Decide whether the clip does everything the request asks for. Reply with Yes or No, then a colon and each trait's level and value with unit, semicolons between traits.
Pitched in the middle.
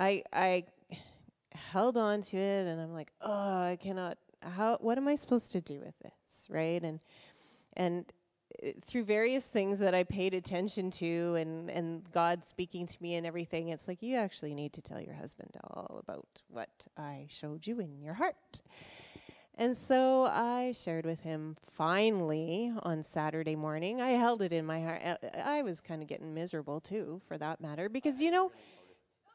Yes: medium, 180 Hz